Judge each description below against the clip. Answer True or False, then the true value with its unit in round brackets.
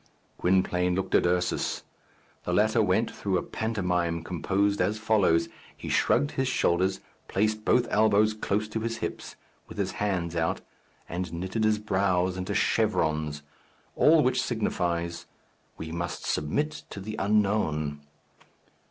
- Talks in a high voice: False (95 Hz)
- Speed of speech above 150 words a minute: False (135 wpm)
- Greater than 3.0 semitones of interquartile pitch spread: True (3.9 semitones)